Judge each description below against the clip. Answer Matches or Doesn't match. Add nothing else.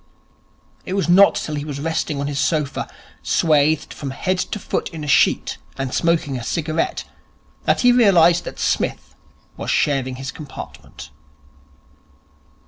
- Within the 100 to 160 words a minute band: Matches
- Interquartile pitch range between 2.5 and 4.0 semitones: Matches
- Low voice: Doesn't match